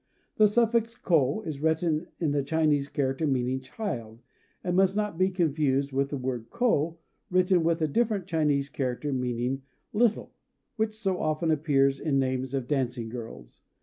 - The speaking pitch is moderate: Yes, medium, 150 Hz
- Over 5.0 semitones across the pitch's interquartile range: Yes, wide, 5.5 semitones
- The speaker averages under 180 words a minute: Yes, average, 170 wpm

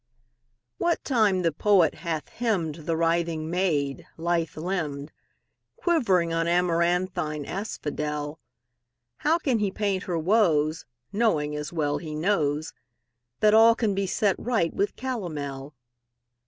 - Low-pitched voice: No, medium, 170 Hz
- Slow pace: Yes, slow, 125 wpm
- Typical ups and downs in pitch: Yes, average, 4.8 semitones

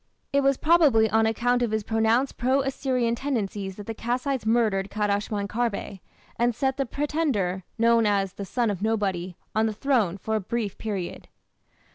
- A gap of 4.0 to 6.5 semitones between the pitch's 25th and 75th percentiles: No, average, 3.5 semitones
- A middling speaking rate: Yes, average, 170 wpm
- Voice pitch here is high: Yes, high, 225 Hz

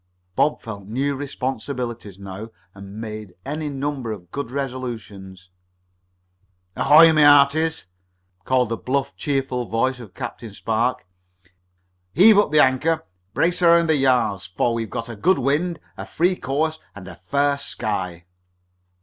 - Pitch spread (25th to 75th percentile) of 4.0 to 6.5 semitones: Yes, average, 5.1 semitones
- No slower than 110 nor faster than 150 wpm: Yes, average, 140 wpm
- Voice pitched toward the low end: Yes, low, 130 Hz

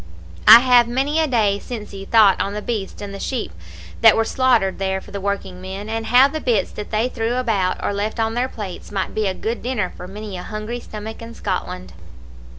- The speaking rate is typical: No, fast, 220 wpm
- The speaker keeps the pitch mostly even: No, average, 3.3 semitones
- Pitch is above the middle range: Yes, high, 215 Hz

